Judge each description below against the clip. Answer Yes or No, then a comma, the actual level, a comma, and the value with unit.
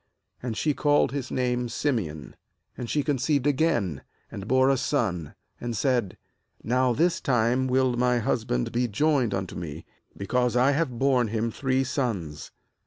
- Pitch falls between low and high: No, low, 125 Hz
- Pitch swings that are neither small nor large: Yes, average, 3.4 semitones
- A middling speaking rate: Yes, average, 155 wpm